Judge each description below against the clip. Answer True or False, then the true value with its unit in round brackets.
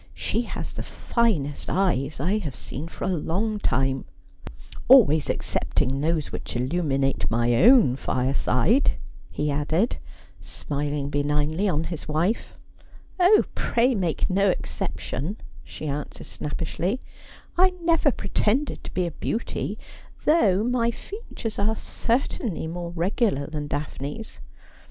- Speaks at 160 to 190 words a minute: False (135 wpm)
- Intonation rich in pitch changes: True (7.3 semitones)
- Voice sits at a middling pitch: True (170 Hz)